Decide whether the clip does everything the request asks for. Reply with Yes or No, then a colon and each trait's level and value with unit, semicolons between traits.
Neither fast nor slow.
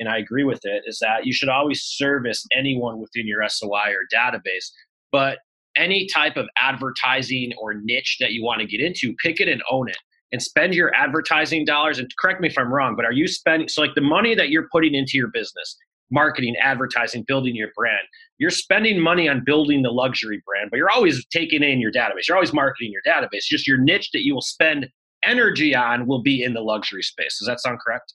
No: fast, 220 wpm